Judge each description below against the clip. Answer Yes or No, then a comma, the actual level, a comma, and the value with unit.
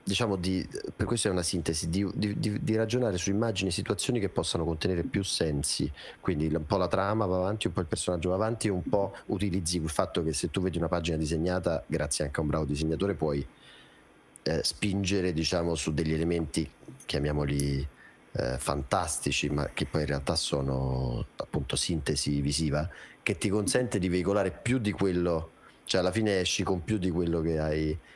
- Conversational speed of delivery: No, fast, 190 wpm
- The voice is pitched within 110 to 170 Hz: No, very low, 85 Hz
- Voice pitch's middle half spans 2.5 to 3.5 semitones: No, average, 4.3 semitones